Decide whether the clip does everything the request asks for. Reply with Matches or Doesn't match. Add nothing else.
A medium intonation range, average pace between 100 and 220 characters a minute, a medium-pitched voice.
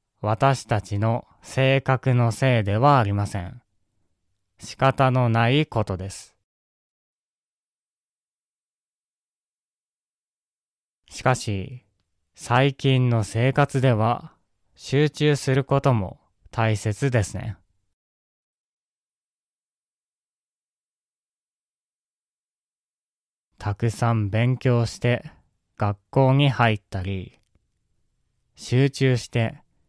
Doesn't match